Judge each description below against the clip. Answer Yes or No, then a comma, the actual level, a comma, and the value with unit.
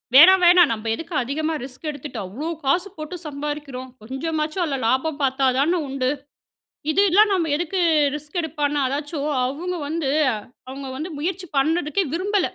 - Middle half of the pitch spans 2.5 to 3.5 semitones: No, average, 4.1 semitones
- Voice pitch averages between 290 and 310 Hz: Yes, very high, 300 Hz